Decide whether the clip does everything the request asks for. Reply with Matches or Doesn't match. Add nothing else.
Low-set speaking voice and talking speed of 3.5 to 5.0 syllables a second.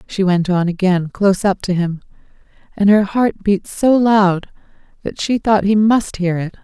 Doesn't match